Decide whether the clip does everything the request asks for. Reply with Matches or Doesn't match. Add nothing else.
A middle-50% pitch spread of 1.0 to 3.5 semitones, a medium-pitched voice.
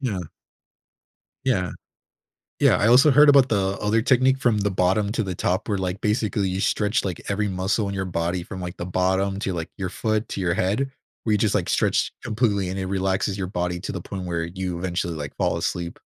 Doesn't match